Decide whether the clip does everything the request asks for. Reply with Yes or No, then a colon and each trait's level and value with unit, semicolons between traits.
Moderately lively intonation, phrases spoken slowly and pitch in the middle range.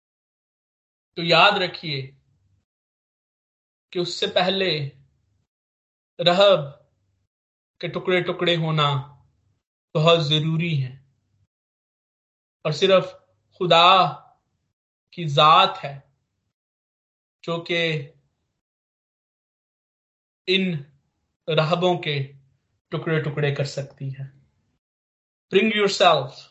Yes: average, 4.6 semitones; slow, 75 wpm; medium, 150 Hz